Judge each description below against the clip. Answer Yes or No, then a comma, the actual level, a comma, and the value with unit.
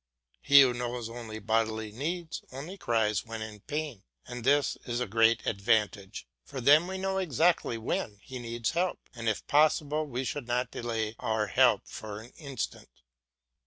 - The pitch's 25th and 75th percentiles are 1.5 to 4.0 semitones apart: No, average, 4.7 semitones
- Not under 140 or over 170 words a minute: Yes, average, 165 wpm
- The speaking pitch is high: No, low, 120 Hz